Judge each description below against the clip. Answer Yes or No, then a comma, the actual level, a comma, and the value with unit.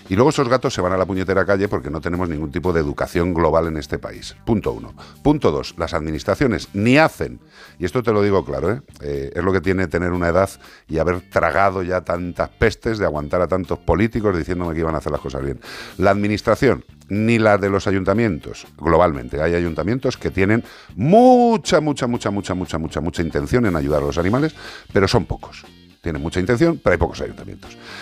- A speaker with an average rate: No, fast, 210 wpm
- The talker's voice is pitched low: Yes, very low, 90 Hz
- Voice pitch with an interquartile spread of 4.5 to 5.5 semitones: No, average, 3.9 semitones